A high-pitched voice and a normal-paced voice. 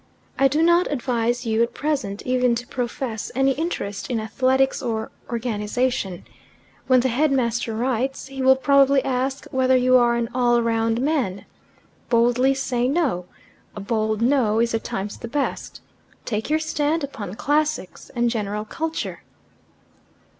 Yes: very high, 250 Hz; average, 145 wpm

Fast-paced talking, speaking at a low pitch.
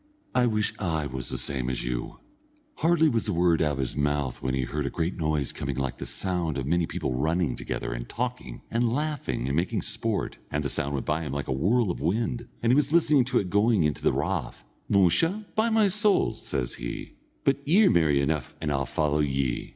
Yes: fast, 220 wpm; very low, 80 Hz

